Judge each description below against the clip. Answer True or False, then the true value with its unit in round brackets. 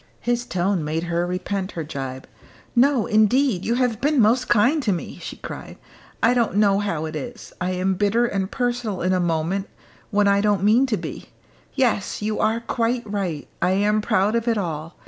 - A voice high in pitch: True (205 Hz)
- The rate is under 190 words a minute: False (195 wpm)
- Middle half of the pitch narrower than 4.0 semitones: False (4.4 semitones)